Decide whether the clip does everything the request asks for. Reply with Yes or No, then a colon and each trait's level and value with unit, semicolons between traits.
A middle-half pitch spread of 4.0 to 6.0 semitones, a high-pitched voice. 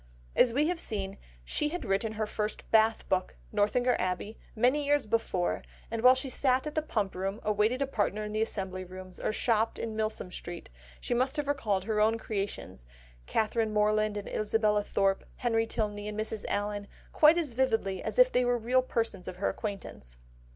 No: average, 3.3 semitones; high, 215 Hz